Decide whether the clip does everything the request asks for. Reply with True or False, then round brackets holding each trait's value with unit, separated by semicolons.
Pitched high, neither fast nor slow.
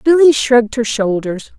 True (245 Hz; 150 wpm)